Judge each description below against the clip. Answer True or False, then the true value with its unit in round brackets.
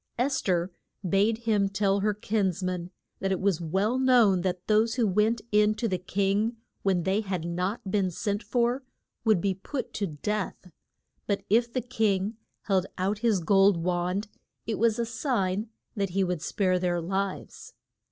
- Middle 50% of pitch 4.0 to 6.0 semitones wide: False (3.0 semitones)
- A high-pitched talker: True (200 Hz)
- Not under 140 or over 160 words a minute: False (170 wpm)